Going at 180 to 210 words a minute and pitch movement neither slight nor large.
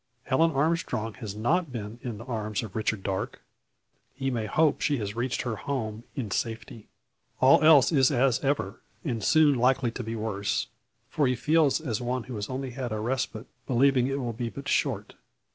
Yes: average, 190 wpm; average, 3.8 semitones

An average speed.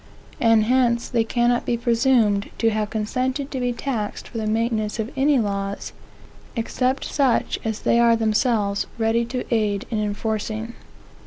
Yes: average, 155 wpm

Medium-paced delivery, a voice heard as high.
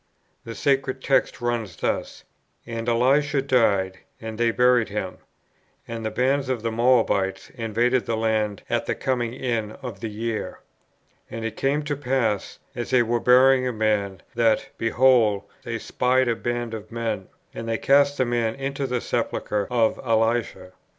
No: average, 165 wpm; low, 115 Hz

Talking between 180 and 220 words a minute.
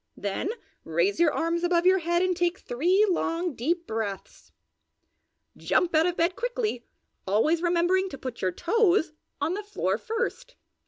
No: average, 155 wpm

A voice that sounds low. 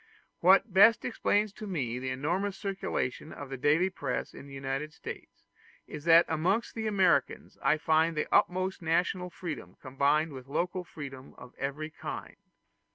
No: medium, 160 Hz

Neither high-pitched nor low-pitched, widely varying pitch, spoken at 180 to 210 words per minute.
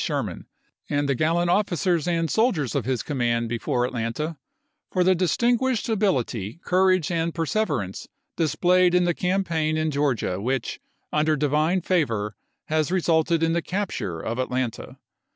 No: medium, 160 Hz; wide, 5.7 semitones; average, 145 wpm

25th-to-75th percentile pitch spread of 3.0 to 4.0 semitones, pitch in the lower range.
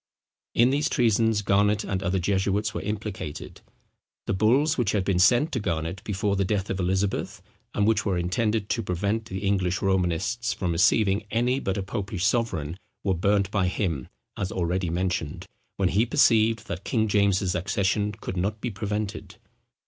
No: narrow, 2.6 semitones; low, 100 Hz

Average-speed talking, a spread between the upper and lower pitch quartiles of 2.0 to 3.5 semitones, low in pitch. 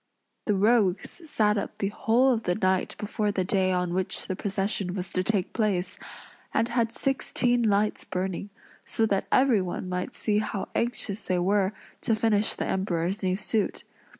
No: average, 170 wpm; average, 2.9 semitones; high, 205 Hz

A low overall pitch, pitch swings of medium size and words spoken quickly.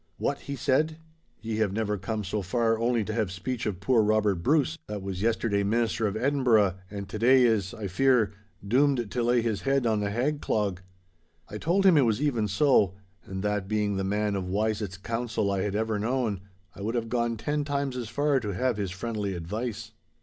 Yes: low, 110 Hz; average, 3.4 semitones; fast, 210 wpm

